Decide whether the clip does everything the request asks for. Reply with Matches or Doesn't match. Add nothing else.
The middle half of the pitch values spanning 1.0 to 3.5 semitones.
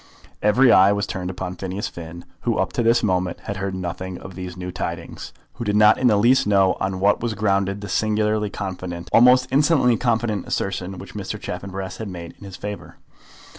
Matches